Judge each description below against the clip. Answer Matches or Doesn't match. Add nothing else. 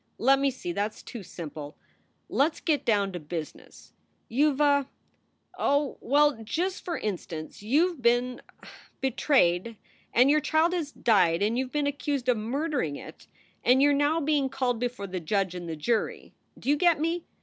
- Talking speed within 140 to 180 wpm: Doesn't match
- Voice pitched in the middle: Doesn't match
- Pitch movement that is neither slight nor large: Doesn't match